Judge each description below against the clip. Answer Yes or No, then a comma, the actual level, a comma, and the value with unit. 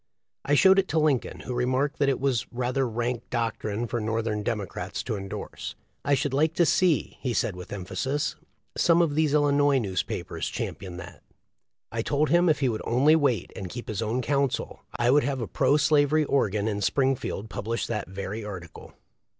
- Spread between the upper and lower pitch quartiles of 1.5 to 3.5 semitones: No, average, 4.9 semitones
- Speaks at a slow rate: No, average, 190 wpm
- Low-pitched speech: Yes, low, 125 Hz